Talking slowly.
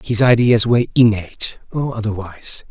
Yes: slow, 110 wpm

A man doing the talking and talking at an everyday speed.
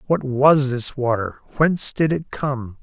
Yes: male; average, 170 wpm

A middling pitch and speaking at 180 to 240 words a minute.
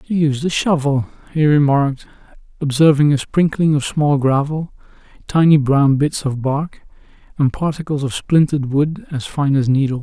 No: medium, 145 Hz; average, 155 wpm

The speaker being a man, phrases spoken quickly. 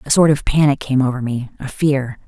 No: female; fast, 240 wpm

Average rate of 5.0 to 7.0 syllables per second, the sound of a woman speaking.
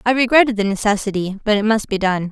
Yes: 6.6 syllables/s; female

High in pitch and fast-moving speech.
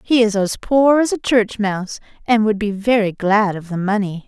Yes: high, 215 Hz; fast, 225 wpm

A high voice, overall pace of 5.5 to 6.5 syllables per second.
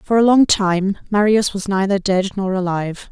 No: high, 195 Hz; 4.9 syllables/s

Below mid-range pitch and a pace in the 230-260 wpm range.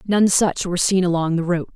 No: medium, 180 Hz; fast, 240 wpm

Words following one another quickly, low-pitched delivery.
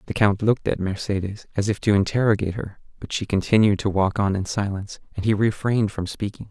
Yes: fast, 210 wpm; low, 100 Hz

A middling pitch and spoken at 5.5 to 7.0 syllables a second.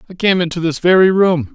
Yes: medium, 175 Hz; 5.8 syllables/s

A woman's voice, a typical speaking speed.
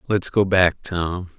No: male; average, 175 wpm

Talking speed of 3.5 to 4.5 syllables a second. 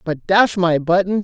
Yes: 4.2 syllables/s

